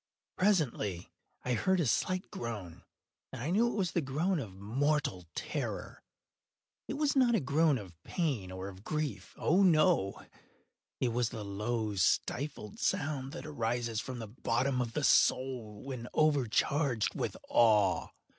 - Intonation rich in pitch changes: Yes, wide, 6.2 semitones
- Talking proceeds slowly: No, average, 145 wpm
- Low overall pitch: Yes, low, 130 Hz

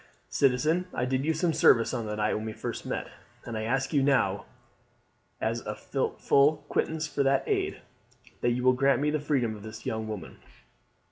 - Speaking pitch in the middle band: No, low, 130 Hz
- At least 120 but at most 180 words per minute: No, average, 195 wpm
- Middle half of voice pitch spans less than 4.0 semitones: No, average, 4.8 semitones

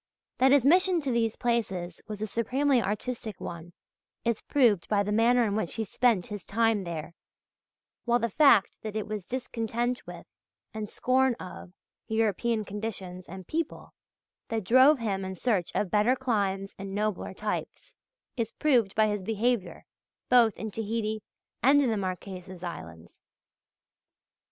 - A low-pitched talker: No, high, 220 Hz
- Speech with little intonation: No, average, 3.7 semitones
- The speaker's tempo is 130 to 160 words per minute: Yes, average, 150 wpm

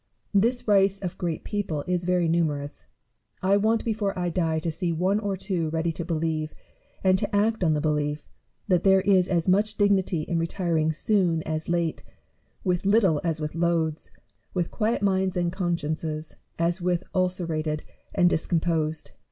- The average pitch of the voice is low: No, medium, 175 Hz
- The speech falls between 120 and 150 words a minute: No, average, 165 wpm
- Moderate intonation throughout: Yes, average, 3.2 semitones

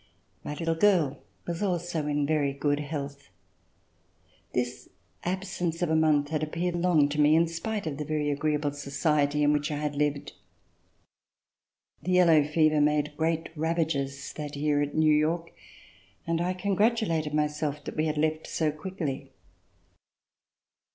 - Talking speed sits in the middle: Yes, average, 150 wpm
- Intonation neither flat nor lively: No, narrow, 2.2 semitones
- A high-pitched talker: No, medium, 155 Hz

